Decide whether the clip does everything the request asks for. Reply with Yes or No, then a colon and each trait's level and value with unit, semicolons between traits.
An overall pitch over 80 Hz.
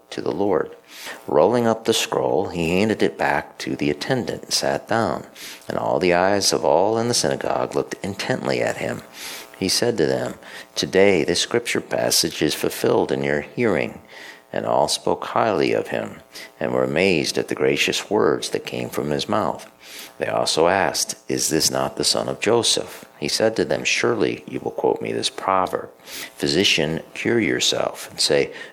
No: very low, 75 Hz